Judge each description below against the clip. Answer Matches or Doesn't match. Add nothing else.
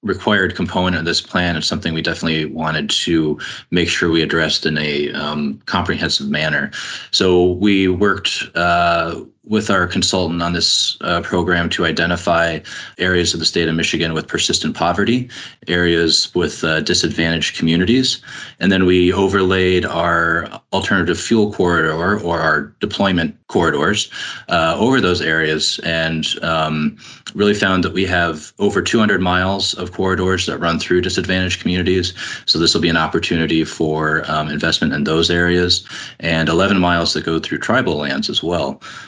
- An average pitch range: Doesn't match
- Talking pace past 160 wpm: Doesn't match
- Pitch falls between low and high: Doesn't match